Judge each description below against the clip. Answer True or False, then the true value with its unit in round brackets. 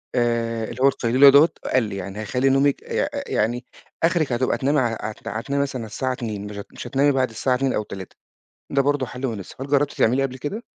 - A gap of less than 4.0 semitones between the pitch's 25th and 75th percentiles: True (3.3 semitones)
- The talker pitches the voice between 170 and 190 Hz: False (130 Hz)